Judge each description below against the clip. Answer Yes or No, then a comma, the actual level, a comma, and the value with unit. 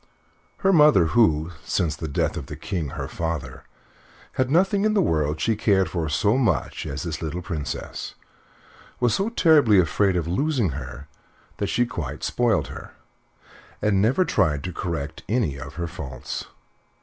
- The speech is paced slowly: No, average, 160 wpm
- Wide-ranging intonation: Yes, wide, 7.8 semitones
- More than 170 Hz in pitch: No, very low, 90 Hz